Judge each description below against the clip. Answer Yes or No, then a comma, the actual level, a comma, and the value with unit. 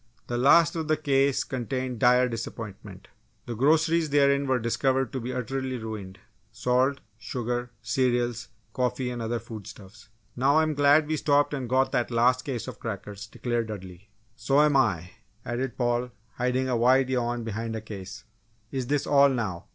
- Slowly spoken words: No, average, 160 wpm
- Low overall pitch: Yes, low, 125 Hz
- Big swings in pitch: No, average, 3.0 semitones